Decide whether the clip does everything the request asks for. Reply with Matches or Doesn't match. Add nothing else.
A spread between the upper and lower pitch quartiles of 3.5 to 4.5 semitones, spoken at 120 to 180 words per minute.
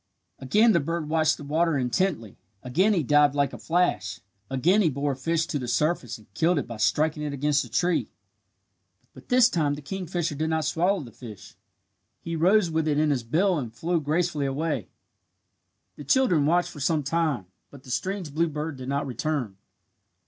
Doesn't match